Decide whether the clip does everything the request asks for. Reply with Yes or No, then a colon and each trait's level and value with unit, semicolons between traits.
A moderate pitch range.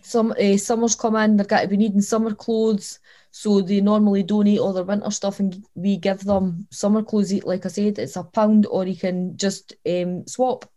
No: narrow, 1.7 semitones